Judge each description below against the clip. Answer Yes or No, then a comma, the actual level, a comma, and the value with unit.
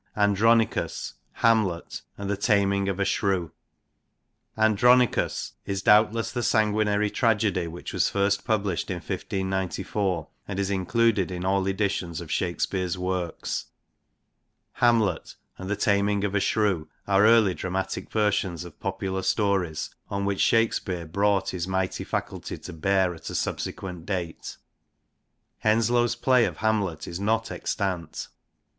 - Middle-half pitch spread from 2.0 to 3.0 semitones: Yes, narrow, 2.5 semitones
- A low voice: Yes, low, 100 Hz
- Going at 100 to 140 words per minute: Yes, slow, 135 wpm